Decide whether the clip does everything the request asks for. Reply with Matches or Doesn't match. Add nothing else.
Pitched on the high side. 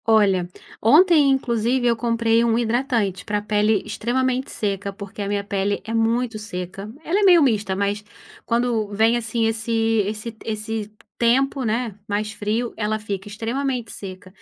Matches